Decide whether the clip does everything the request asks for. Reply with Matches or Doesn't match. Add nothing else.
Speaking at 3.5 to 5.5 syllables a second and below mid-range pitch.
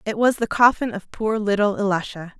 Doesn't match